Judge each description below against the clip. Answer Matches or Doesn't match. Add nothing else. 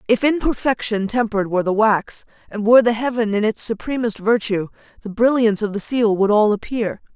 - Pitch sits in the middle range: Doesn't match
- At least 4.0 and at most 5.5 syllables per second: Doesn't match